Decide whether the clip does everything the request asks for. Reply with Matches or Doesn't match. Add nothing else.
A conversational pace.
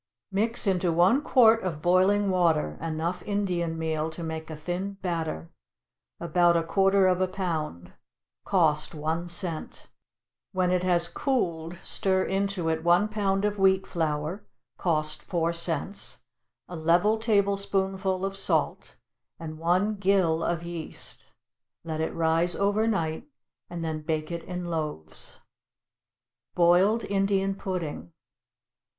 Doesn't match